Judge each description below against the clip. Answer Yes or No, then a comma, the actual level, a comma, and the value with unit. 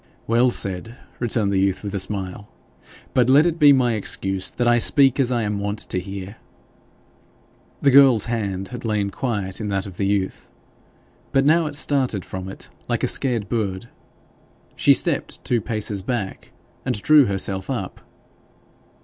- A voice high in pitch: No, low, 110 Hz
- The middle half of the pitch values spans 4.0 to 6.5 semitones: Yes, average, 4.3 semitones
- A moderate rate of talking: Yes, average, 165 wpm